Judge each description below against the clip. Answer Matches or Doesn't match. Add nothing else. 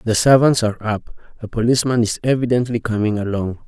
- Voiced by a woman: Doesn't match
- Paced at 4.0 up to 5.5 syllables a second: Doesn't match